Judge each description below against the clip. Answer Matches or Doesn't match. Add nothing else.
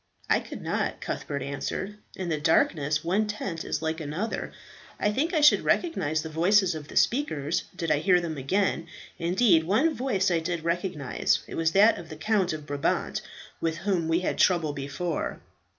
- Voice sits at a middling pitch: Matches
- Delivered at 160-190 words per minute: Matches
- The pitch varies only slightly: Doesn't match